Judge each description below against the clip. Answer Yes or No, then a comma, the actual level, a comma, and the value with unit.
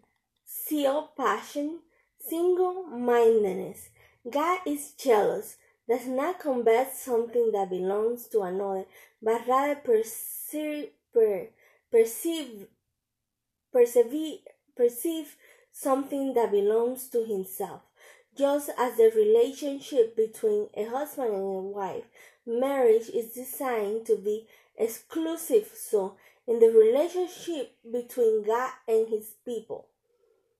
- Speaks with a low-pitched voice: No, very high, 290 Hz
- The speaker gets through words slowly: Yes, slow, 100 wpm